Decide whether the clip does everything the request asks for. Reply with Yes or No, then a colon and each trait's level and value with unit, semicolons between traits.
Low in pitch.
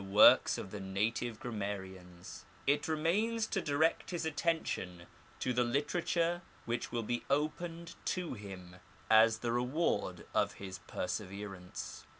Yes: low, 120 Hz